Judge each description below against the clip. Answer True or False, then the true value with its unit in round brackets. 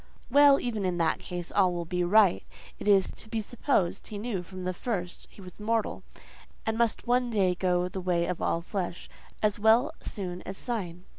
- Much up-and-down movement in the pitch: False (3.7 semitones)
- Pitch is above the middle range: True (195 Hz)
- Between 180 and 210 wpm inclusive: True (200 wpm)